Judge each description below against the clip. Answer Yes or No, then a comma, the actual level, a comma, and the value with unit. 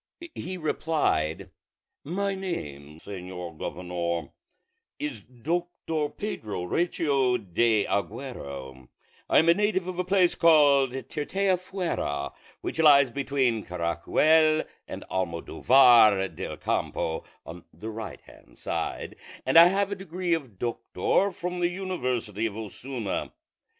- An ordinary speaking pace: No, slow, 115 wpm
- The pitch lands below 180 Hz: Yes, low, 135 Hz